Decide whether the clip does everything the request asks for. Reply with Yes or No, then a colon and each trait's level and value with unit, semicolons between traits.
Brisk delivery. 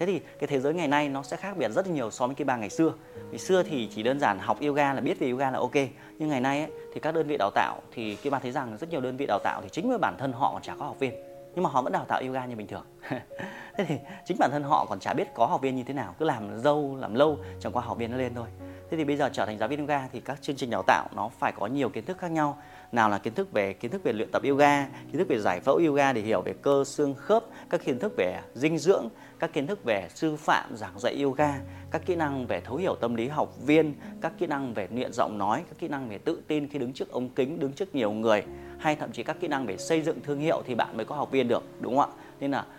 Yes: fast, 305 wpm